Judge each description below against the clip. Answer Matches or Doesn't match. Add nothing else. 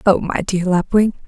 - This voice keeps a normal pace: Matches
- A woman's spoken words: Matches